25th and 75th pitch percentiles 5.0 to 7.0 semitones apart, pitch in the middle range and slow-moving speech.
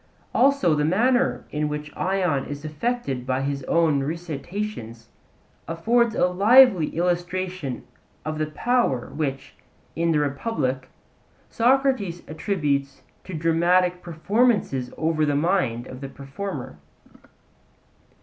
Yes: wide, 5.5 semitones; medium, 165 Hz; slow, 110 wpm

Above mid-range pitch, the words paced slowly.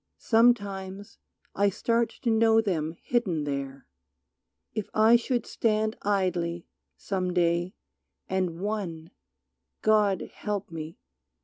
Yes: high, 195 Hz; slow, 105 wpm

